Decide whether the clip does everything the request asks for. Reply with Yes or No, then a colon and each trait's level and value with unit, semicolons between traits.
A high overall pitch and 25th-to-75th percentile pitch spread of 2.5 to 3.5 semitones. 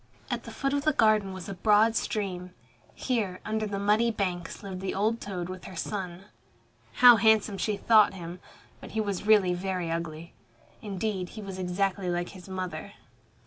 Yes: high, 195 Hz; average, 2.9 semitones